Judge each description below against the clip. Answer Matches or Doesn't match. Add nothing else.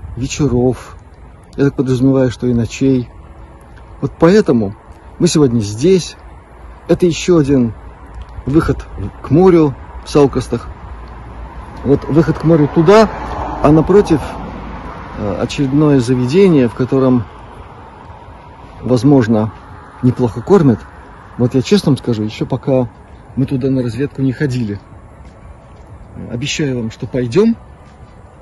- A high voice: Doesn't match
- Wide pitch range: Matches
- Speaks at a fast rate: Doesn't match